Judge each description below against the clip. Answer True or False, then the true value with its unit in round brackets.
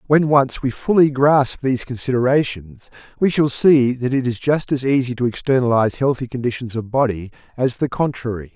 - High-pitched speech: False (130 Hz)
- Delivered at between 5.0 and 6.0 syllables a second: True (5.3 syllables/s)